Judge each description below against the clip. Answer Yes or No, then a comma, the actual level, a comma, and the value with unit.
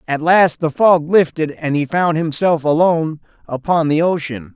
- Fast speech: No, average, 170 wpm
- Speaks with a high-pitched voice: No, medium, 160 Hz